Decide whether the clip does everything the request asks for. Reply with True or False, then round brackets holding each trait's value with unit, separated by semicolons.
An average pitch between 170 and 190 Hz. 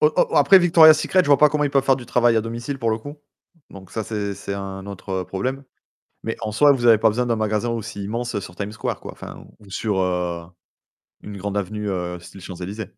False (110 Hz)